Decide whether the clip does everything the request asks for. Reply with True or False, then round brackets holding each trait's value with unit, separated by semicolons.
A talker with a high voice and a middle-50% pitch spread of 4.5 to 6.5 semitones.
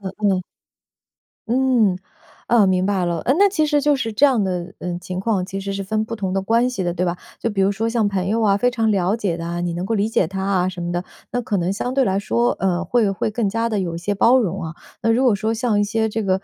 False (200 Hz; 3.6 semitones)